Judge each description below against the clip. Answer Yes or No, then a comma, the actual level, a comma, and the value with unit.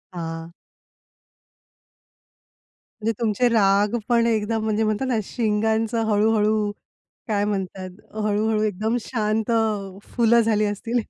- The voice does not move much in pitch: Yes, narrow, 1.6 semitones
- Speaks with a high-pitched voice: Yes, high, 215 Hz